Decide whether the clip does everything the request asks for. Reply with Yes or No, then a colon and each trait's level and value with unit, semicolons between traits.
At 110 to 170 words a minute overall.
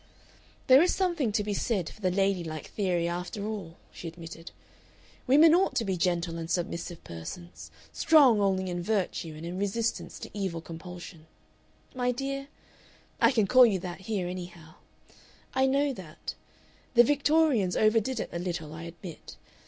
Yes: average, 165 wpm